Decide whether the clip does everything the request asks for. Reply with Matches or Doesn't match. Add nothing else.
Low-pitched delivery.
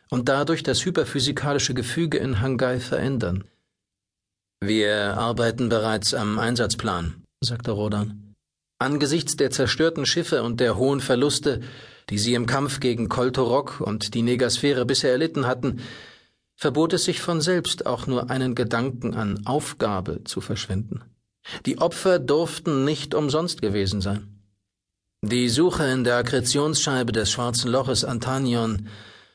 Matches